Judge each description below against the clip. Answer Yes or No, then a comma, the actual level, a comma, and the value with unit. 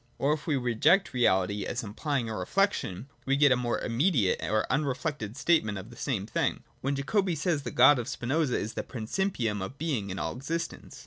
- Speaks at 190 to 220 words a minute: Yes, average, 200 wpm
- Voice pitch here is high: No, low, 130 Hz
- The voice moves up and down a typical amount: No, wide, 5.7 semitones